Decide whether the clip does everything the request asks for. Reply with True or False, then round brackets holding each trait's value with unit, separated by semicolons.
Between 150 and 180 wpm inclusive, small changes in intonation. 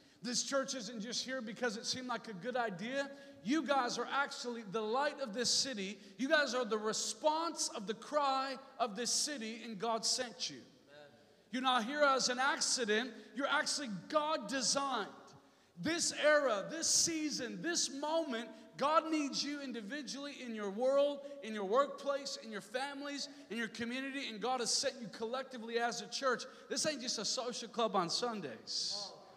False (175 wpm; 3.5 semitones)